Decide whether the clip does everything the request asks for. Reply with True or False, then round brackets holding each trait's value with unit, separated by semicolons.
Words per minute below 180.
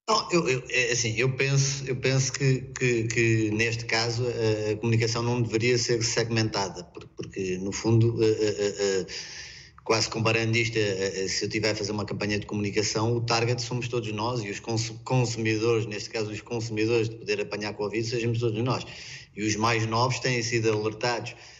False (185 wpm)